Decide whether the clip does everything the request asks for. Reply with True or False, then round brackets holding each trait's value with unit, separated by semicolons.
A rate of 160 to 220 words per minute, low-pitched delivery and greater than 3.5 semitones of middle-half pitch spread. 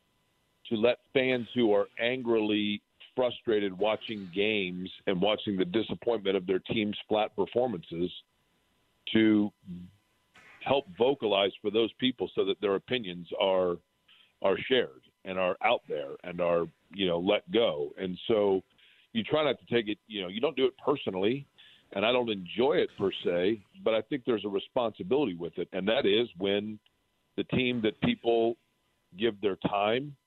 True (165 wpm; 105 Hz; 4.0 semitones)